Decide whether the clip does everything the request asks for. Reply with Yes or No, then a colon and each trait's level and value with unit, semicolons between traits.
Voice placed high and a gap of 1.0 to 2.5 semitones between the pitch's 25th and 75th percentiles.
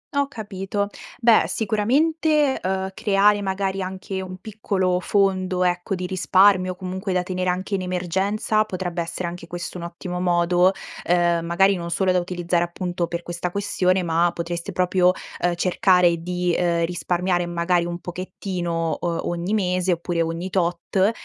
No: medium, 180 Hz; narrow, 1.8 semitones